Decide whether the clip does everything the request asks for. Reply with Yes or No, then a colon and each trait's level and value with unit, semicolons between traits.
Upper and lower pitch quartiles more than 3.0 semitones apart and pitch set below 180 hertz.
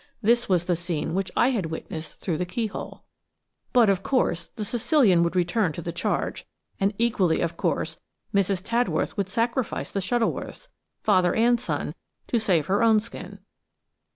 No: average, 4.8 semitones; high, 200 Hz